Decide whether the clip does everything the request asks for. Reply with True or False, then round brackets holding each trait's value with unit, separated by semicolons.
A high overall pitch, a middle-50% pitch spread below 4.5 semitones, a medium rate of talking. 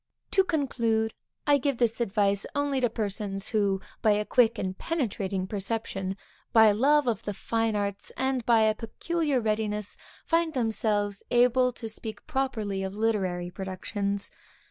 True (220 Hz; 3.7 semitones; 155 wpm)